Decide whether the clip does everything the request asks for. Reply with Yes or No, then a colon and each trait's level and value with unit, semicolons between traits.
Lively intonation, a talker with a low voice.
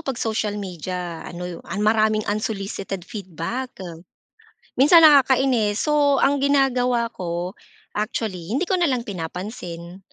No: wide, 6.4 semitones; high, 215 Hz